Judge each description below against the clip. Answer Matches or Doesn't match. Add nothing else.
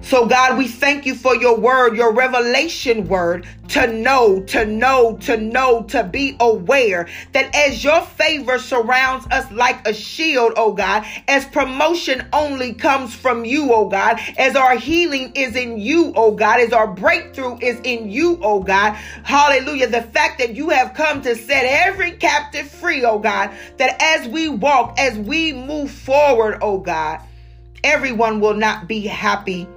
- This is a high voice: Matches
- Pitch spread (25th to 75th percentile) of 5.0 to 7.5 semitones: Doesn't match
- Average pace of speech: Matches